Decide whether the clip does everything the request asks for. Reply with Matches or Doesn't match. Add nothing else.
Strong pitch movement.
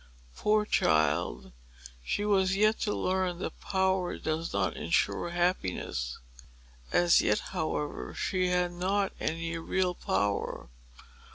Matches